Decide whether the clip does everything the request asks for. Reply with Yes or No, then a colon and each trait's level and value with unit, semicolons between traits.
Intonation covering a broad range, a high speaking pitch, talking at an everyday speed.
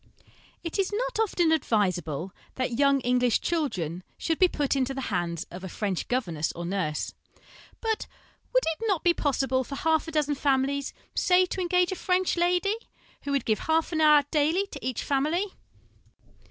Yes: wide, 6.6 semitones; very high, 285 Hz; average, 175 wpm